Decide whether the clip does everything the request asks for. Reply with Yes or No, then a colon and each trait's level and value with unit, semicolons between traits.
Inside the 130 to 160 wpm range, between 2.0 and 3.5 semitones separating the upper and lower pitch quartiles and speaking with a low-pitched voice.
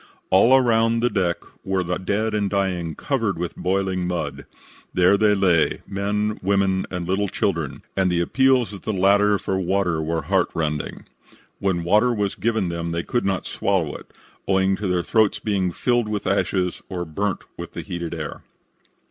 No: average, 180 wpm; average, 2.8 semitones; very low, 95 Hz